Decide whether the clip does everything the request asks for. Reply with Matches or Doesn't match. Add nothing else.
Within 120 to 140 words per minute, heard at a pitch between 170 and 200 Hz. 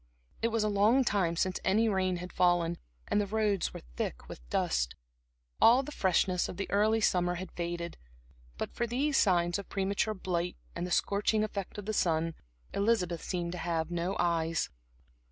Doesn't match